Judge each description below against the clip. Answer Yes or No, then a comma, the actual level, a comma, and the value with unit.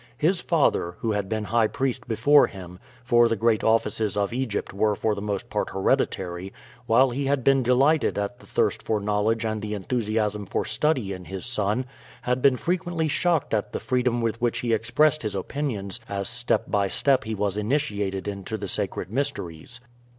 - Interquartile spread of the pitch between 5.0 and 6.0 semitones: No, average, 3.9 semitones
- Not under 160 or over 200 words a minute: Yes, average, 185 wpm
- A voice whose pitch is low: Yes, low, 110 Hz